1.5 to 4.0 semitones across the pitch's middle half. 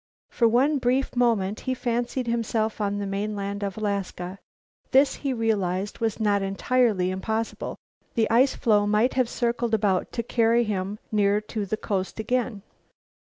Yes: average, 3.0 semitones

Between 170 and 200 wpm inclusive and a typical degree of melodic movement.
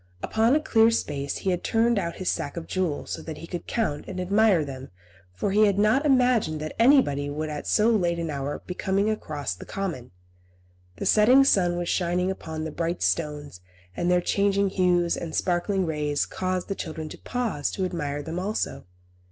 Yes: average, 195 wpm; average, 4.9 semitones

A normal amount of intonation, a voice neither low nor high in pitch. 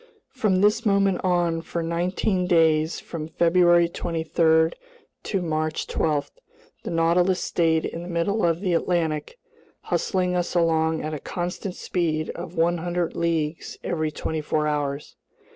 No: narrow, 1.9 semitones; medium, 170 Hz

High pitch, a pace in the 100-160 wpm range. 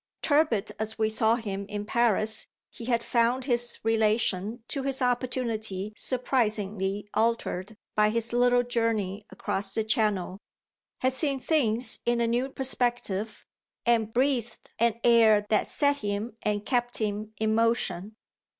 Yes: high, 225 Hz; average, 140 wpm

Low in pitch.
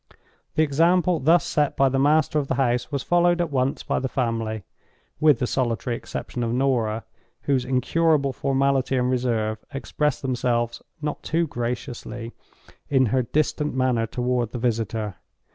Yes: low, 130 Hz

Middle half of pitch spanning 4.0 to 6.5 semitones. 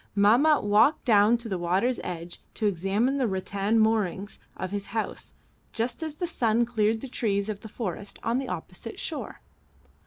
No: average, 3.2 semitones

